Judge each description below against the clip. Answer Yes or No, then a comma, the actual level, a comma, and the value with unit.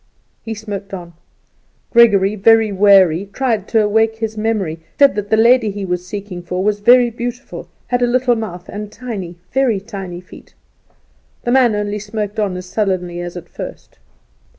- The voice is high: Yes, high, 210 Hz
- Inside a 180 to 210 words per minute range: No, average, 170 wpm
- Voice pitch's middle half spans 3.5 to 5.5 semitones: No, average, 3.0 semitones